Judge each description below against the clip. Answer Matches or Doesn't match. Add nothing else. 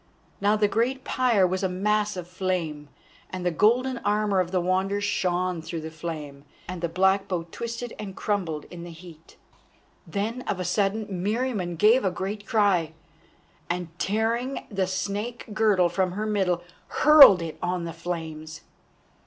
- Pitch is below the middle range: Doesn't match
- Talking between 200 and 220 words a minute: Doesn't match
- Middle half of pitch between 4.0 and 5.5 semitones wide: Doesn't match